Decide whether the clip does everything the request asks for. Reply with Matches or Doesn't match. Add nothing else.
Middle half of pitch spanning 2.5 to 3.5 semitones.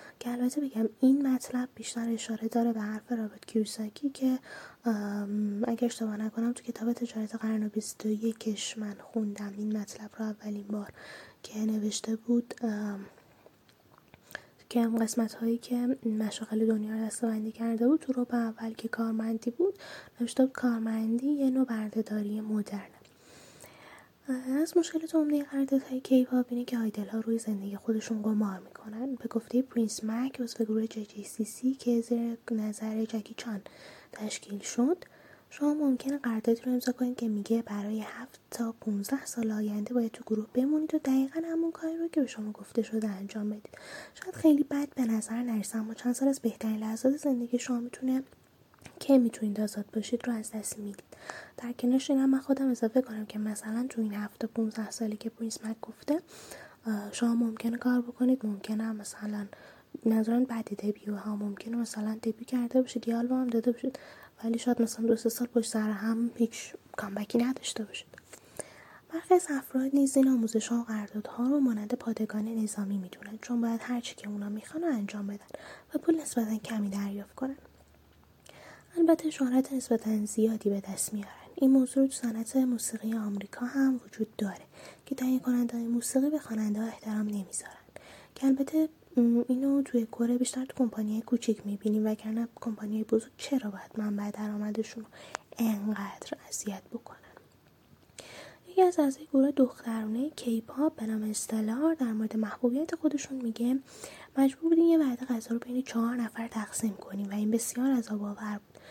Matches